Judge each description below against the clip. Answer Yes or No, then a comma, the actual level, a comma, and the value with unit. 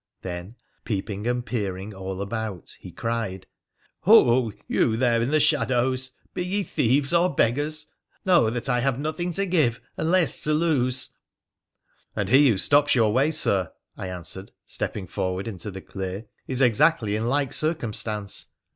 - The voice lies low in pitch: Yes, low, 120 Hz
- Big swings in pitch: Yes, wide, 6.2 semitones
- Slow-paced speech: No, average, 170 wpm